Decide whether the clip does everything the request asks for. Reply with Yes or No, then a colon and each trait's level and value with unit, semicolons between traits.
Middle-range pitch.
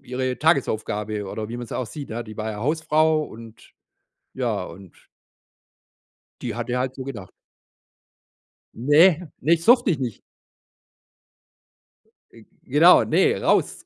No: low, 125 Hz